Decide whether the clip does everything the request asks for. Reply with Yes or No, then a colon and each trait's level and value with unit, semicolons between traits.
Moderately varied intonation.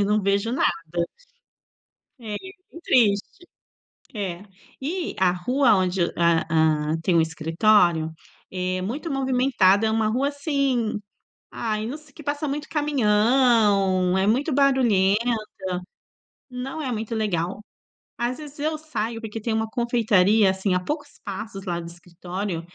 No: wide, 6.0 semitones